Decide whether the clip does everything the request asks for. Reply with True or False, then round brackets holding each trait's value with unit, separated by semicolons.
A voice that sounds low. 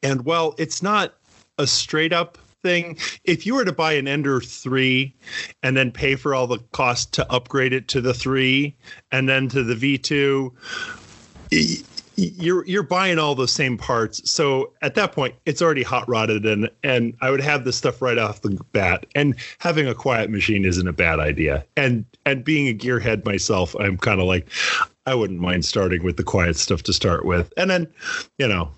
True (130 Hz)